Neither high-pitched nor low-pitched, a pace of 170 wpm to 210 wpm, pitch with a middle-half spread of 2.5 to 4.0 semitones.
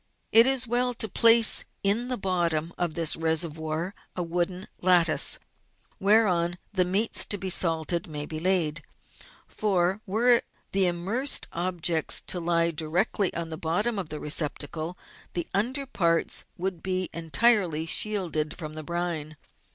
No: medium, 175 Hz; average, 145 wpm; average, 3.5 semitones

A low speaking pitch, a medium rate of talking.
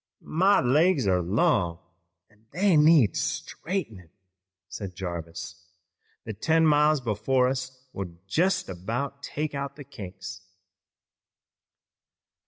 No: low, 125 Hz; slow, 105 wpm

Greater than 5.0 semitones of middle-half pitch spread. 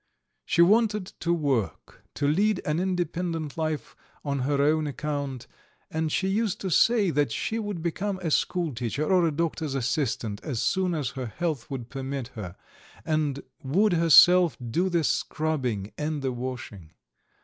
No: average, 4.7 semitones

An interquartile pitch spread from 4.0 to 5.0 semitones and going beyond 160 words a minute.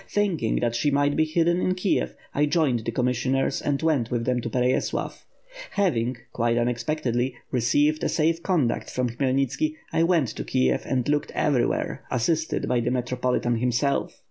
Yes: average, 4.4 semitones; average, 170 wpm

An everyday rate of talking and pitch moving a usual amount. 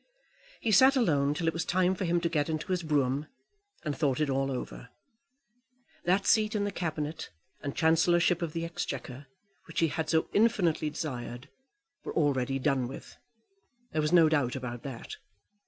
Yes: average, 170 wpm; average, 3.8 semitones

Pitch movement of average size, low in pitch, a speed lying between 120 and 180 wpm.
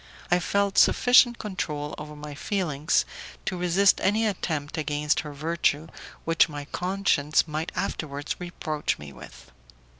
No: average, 4.2 semitones; medium, 155 Hz; average, 140 wpm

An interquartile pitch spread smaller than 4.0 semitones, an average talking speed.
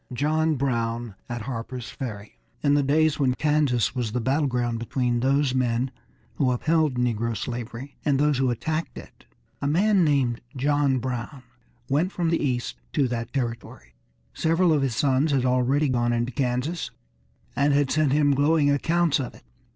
Yes: average, 3.4 semitones; average, 170 wpm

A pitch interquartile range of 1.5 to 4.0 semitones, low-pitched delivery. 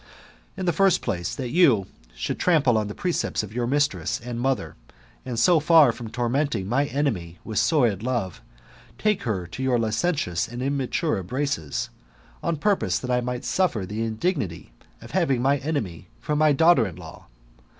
No: wide, 5.6 semitones; low, 125 Hz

